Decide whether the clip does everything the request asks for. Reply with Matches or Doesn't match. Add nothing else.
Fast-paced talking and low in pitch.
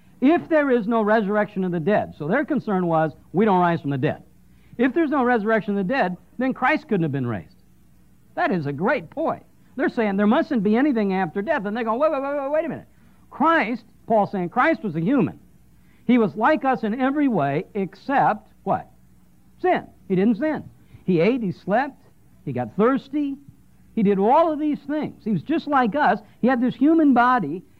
Doesn't match